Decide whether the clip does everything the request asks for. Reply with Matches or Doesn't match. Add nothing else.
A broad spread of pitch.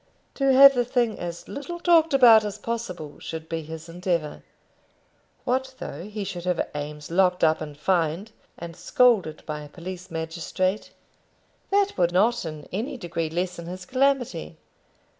Matches